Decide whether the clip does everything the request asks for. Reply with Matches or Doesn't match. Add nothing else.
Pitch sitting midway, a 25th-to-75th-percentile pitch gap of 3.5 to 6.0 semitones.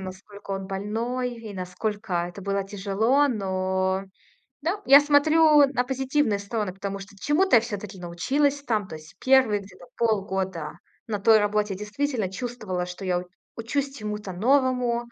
Doesn't match